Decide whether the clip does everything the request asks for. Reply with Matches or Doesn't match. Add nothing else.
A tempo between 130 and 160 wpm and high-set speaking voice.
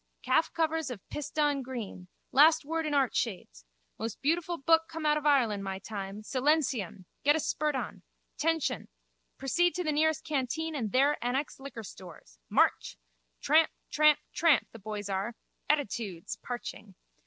Matches